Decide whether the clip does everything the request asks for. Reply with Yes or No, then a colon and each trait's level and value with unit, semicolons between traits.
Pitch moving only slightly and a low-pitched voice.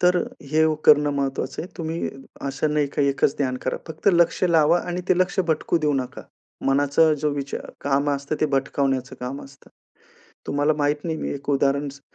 No: narrow, 2.3 semitones; medium, 145 Hz